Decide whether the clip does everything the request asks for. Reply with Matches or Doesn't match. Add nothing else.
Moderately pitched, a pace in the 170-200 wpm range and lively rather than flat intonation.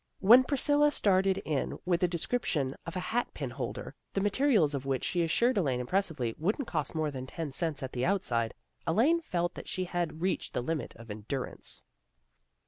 Matches